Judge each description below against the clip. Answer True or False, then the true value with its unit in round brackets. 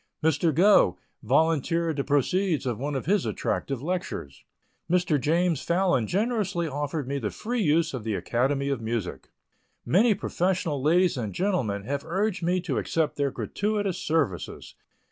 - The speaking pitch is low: False (160 Hz)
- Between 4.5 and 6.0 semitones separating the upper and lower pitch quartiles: True (5.0 semitones)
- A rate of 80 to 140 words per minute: False (150 wpm)